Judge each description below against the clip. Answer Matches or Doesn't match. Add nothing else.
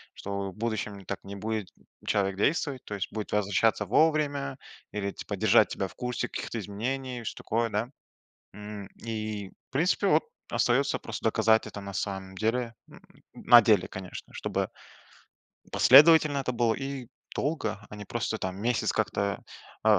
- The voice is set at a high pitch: Doesn't match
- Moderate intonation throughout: Matches